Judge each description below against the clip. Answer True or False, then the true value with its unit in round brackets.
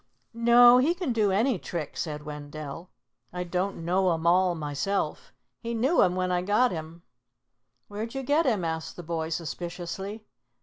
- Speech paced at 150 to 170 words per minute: True (165 wpm)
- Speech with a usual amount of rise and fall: False (5.7 semitones)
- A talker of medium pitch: True (180 Hz)